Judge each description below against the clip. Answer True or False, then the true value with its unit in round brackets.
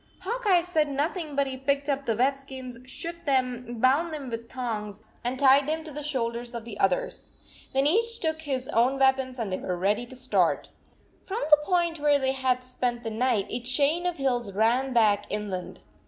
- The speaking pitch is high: True (265 Hz)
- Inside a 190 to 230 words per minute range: True (205 wpm)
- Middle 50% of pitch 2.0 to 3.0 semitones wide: False (3.8 semitones)